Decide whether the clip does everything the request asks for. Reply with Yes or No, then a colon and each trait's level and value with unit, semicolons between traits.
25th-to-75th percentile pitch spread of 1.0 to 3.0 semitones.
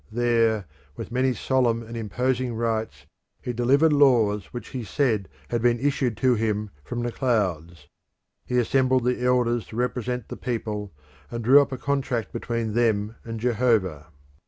Yes: narrow, 2.4 semitones